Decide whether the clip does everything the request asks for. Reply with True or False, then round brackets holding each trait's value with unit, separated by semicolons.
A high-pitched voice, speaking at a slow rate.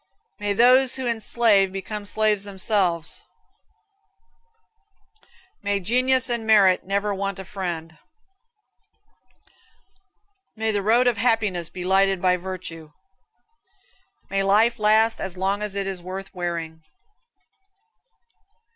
True (200 Hz; 110 wpm)